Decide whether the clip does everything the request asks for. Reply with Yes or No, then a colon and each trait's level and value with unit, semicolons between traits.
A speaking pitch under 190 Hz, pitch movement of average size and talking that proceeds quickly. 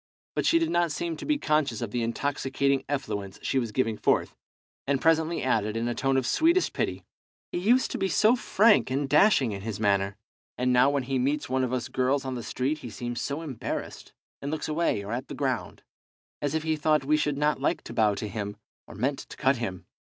Yes: low, 135 Hz; average, 4.5 semitones; fast, 230 wpm